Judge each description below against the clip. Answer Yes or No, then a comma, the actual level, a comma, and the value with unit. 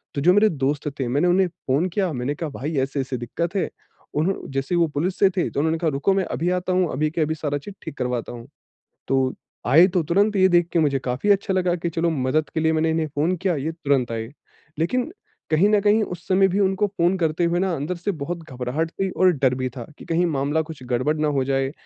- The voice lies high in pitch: No, medium, 160 Hz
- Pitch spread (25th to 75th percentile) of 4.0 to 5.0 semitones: Yes, average, 4.6 semitones